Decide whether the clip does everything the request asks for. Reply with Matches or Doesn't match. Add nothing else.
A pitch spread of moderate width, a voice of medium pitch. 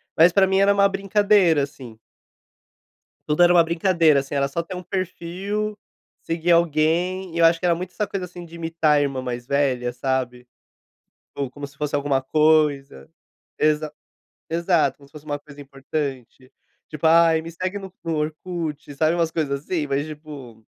Matches